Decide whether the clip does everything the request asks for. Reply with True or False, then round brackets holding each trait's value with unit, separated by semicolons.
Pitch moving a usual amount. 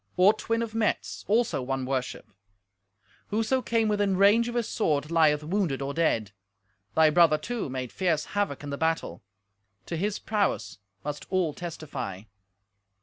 False (6.6 semitones)